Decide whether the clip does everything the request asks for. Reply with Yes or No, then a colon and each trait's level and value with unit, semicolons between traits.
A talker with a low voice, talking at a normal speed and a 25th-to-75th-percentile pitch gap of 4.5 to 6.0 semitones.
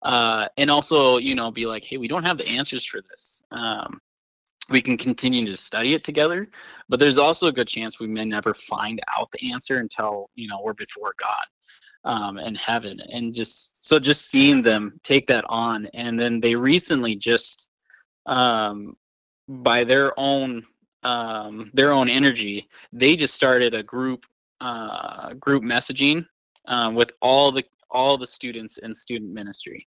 No: low, 120 Hz; average, 170 wpm; average, 3.4 semitones